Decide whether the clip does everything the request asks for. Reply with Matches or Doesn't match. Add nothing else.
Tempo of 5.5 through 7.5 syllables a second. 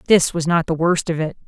Matches